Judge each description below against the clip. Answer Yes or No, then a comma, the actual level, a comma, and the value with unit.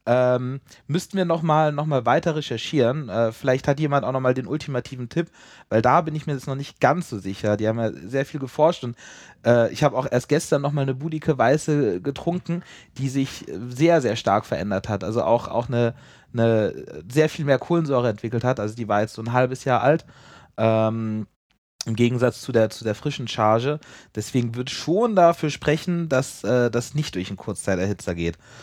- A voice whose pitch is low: Yes, low, 130 Hz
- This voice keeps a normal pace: No, fast, 200 wpm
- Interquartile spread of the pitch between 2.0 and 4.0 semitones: No, average, 4.5 semitones